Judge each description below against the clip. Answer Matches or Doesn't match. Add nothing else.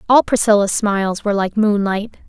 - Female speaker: Matches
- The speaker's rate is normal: Matches